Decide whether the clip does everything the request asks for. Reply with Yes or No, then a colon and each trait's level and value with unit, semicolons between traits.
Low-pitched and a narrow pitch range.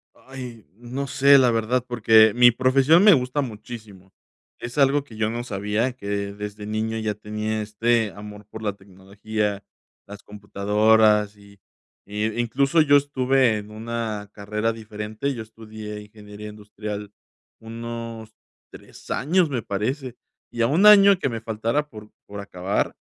No: low, 110 Hz; average, 3.1 semitones